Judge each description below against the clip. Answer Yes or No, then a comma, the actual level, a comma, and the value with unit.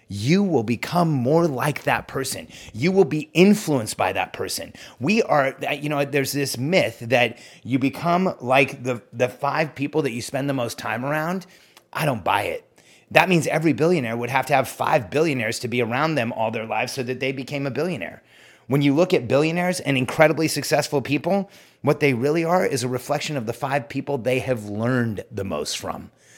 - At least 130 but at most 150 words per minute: No, average, 200 wpm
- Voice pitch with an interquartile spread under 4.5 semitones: Yes, average, 3.7 semitones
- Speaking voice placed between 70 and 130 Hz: No, medium, 140 Hz